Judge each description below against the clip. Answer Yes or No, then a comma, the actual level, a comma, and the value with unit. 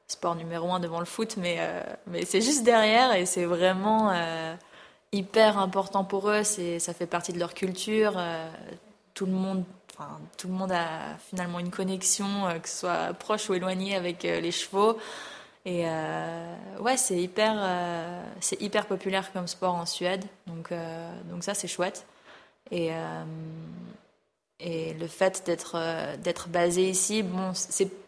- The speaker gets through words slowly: No, average, 170 wpm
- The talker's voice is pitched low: No, medium, 185 Hz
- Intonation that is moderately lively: No, narrow, 2.3 semitones